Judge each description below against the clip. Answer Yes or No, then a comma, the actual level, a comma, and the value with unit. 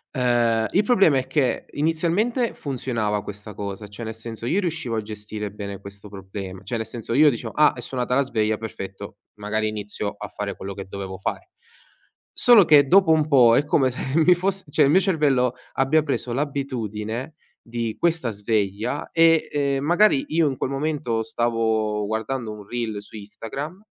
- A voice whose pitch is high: No, low, 120 Hz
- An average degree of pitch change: No, wide, 5.8 semitones